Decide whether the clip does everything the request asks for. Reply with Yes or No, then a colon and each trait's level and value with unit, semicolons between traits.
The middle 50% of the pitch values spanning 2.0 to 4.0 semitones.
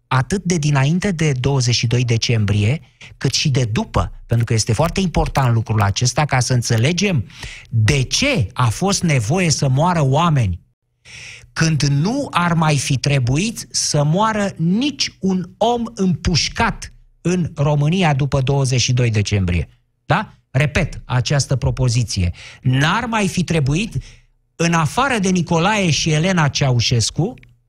No: wide, 5.5 semitones